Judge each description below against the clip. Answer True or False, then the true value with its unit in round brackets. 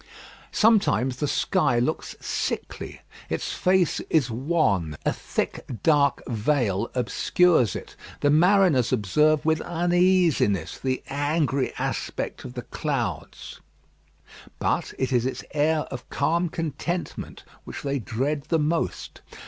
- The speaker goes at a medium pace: False (120 wpm)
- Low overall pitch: False (145 Hz)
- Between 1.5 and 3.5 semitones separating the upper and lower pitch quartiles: False (5.0 semitones)